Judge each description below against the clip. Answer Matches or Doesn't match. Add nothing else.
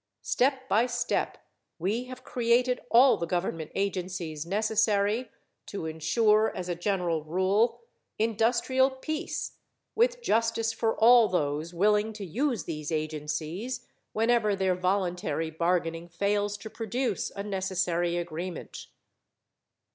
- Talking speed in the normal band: Doesn't match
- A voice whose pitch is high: Matches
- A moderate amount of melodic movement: Matches